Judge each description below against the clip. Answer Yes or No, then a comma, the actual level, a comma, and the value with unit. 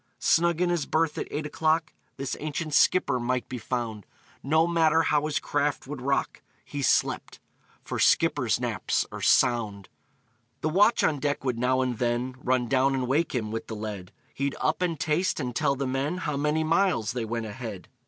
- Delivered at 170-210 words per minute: Yes, average, 190 wpm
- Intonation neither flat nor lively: Yes, average, 4.2 semitones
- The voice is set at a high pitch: No, medium, 140 Hz